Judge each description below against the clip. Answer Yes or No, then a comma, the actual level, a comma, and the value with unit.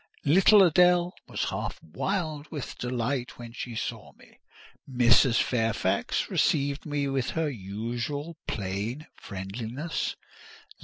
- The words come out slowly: Yes, slow, 110 wpm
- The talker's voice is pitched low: Yes, low, 130 Hz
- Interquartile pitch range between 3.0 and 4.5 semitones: No, average, 5.1 semitones